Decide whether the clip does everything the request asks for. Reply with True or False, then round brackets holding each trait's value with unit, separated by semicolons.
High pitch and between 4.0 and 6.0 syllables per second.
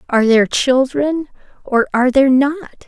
True (265 Hz; 5.3 syllables/s)